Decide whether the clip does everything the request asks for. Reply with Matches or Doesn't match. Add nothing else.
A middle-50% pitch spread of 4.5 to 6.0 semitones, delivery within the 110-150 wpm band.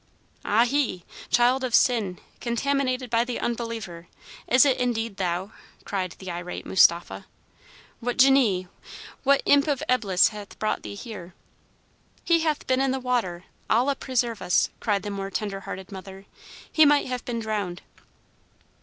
Matches